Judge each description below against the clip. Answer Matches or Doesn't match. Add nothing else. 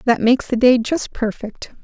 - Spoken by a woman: Matches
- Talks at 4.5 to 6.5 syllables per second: Matches